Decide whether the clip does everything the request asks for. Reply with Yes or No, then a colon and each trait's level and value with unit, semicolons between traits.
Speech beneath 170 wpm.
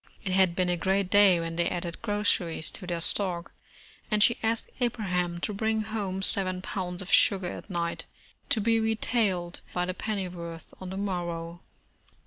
No: average, 175 wpm